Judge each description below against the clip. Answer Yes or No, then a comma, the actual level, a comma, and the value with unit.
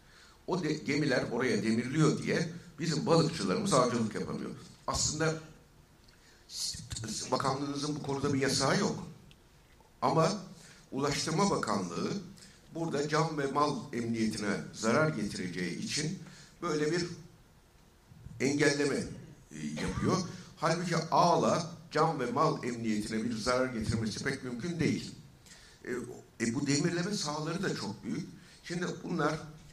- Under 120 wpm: Yes, average, 110 wpm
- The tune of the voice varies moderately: Yes, average, 4.3 semitones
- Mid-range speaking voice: Yes, medium, 150 Hz